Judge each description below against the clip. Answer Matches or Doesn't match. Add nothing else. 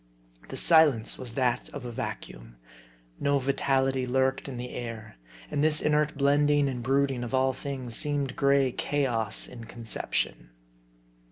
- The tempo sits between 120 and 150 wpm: Matches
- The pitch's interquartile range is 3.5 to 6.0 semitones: Doesn't match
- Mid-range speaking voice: Doesn't match